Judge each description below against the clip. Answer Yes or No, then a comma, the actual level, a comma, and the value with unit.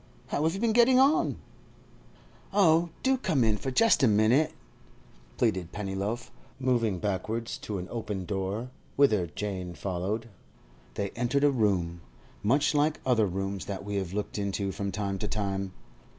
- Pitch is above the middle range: No, low, 105 Hz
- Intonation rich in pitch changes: Yes, wide, 5.8 semitones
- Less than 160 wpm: Yes, average, 150 wpm